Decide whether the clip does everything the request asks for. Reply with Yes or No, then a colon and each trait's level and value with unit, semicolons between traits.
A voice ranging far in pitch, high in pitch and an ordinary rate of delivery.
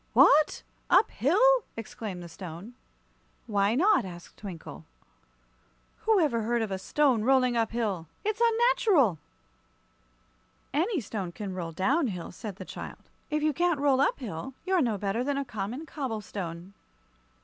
Yes: wide, 7.5 semitones; high, 235 Hz; average, 150 wpm